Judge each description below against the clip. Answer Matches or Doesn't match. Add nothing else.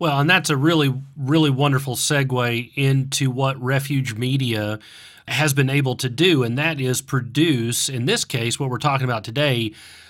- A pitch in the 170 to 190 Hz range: Doesn't match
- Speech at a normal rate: Matches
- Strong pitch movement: Doesn't match